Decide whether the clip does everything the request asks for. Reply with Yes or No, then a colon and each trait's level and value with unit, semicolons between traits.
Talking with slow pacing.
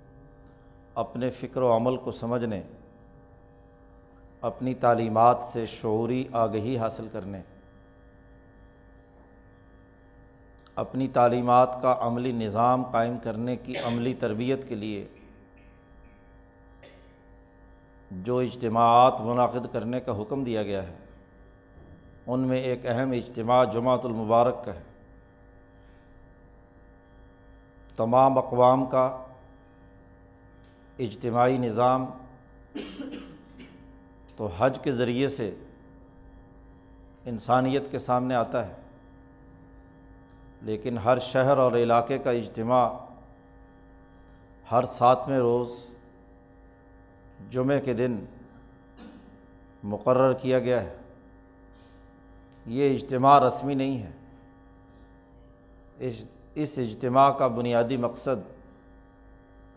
Yes: slow, 85 wpm